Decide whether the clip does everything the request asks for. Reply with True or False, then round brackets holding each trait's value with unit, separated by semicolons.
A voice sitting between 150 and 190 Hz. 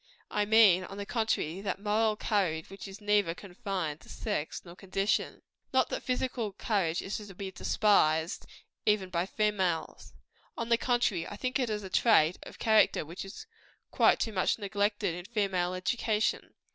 False (200 Hz)